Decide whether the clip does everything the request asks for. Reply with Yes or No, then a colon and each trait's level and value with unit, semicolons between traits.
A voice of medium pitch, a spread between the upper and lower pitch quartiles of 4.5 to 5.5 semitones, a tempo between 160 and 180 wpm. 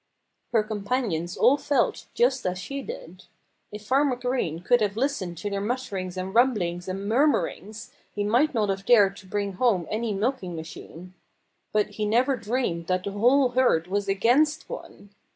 No: high, 210 Hz; average, 5.0 semitones; average, 165 wpm